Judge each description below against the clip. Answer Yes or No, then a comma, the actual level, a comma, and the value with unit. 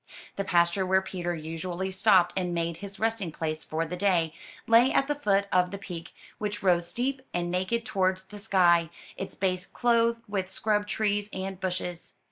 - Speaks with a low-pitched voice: No, high, 190 Hz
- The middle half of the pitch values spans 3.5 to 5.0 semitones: No, average, 2.9 semitones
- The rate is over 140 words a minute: Yes, average, 180 wpm